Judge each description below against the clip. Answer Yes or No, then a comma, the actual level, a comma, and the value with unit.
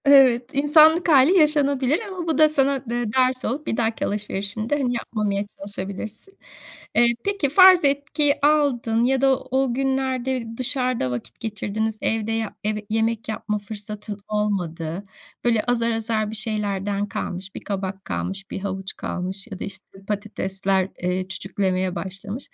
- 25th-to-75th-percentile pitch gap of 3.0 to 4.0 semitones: No, average, 5.1 semitones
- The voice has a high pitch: Yes, high, 225 Hz